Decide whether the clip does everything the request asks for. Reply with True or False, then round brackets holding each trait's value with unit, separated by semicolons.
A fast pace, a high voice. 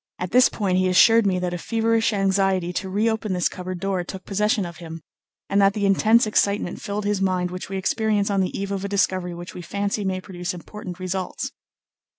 True (215 wpm; 195 Hz)